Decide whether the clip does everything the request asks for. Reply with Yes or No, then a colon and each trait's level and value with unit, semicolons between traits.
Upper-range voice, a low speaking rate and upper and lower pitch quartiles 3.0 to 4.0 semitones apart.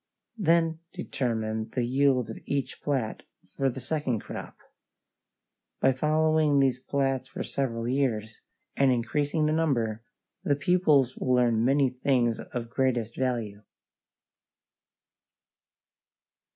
No: low, 130 Hz; slow, 110 wpm; average, 3.3 semitones